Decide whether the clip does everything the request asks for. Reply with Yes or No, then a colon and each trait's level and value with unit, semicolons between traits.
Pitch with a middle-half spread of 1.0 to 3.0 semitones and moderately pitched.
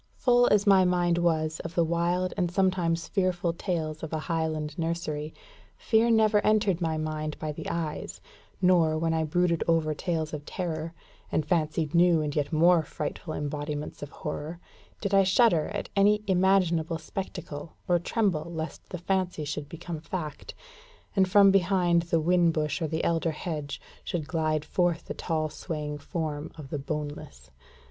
Yes: narrow, 2.6 semitones; medium, 165 Hz